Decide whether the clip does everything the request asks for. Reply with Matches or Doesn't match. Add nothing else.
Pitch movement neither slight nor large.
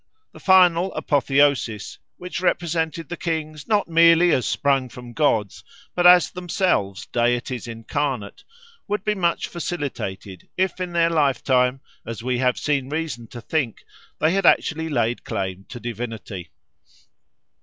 Doesn't match